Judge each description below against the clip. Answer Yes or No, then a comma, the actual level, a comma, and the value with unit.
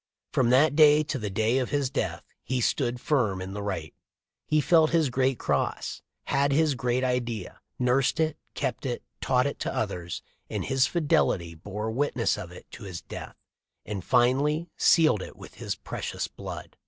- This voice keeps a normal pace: Yes, average, 180 wpm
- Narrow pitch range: No, average, 5.2 semitones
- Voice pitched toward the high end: No, low, 125 Hz